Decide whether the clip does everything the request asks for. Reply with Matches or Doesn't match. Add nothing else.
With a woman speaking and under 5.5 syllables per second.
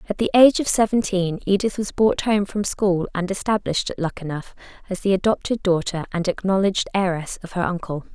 Doesn't match